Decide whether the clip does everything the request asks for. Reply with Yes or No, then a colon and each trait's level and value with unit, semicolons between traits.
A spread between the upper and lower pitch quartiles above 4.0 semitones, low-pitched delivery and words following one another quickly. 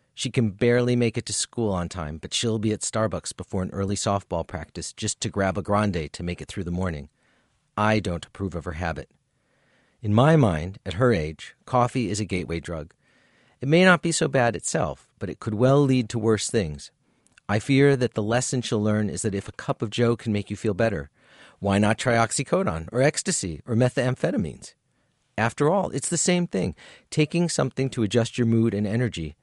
Yes: average, 4.7 semitones; low, 110 Hz; fast, 210 wpm